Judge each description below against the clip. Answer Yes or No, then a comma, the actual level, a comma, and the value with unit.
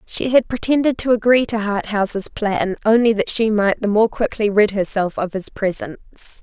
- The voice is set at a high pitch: Yes, high, 215 Hz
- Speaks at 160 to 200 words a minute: Yes, average, 185 wpm